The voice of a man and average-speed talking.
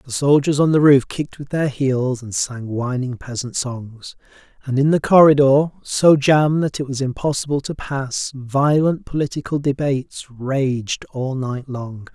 Yes: male; average, 165 wpm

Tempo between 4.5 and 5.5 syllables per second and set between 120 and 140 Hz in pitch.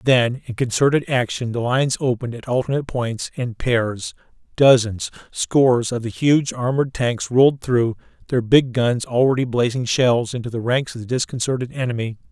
Yes: 5.2 syllables/s; low, 125 Hz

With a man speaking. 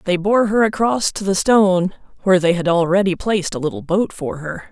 No: female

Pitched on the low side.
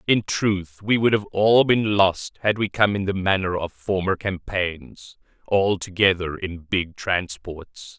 Yes: very low, 95 Hz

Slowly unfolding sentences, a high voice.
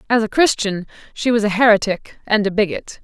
No: average, 200 wpm; high, 215 Hz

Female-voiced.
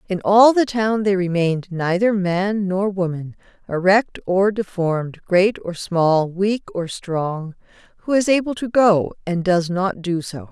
Yes: female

